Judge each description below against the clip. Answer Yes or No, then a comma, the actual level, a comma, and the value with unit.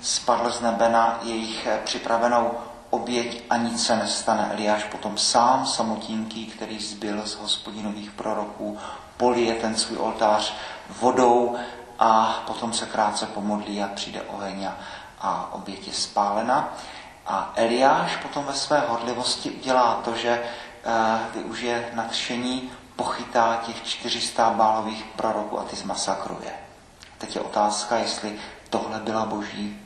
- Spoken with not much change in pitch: Yes, narrow, 1.8 semitones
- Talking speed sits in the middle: Yes, average, 125 wpm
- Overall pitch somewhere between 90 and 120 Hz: Yes, low, 115 Hz